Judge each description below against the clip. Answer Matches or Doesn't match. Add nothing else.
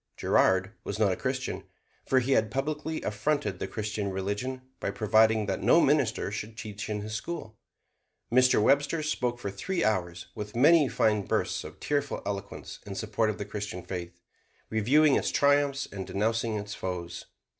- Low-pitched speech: Matches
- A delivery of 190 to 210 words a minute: Doesn't match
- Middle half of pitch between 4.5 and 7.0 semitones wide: Matches